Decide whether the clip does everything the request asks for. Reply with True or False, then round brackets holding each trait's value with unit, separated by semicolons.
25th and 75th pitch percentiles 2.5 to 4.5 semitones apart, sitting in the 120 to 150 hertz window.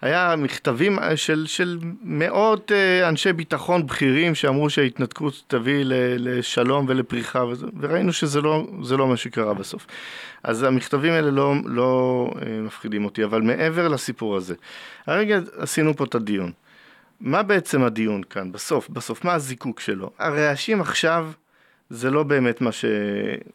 False (5.1 semitones; 140 Hz)